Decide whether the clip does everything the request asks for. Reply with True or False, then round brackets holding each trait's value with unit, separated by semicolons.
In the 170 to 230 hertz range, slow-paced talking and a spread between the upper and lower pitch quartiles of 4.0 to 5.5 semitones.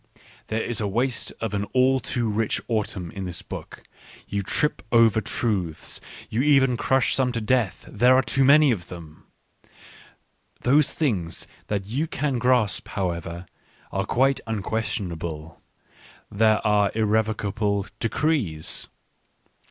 False (110 Hz; 130 wpm; 4.6 semitones)